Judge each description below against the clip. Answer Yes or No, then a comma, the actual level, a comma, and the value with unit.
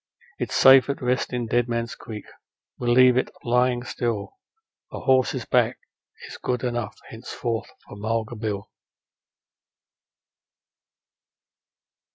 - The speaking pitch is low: Yes, low, 120 Hz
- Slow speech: Yes, slow, 115 wpm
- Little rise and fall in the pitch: Yes, narrow, 1.8 semitones